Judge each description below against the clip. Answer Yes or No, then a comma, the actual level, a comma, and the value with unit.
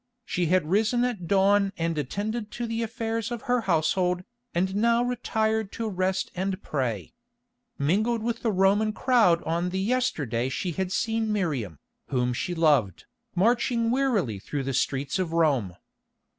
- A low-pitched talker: No, high, 190 Hz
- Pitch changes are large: Yes, wide, 5.8 semitones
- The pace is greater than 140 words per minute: Yes, average, 155 wpm